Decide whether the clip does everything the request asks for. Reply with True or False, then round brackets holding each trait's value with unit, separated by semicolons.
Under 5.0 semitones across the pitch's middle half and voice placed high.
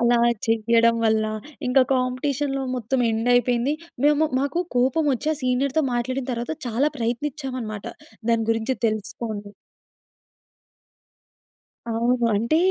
True (2.8 semitones; 245 Hz)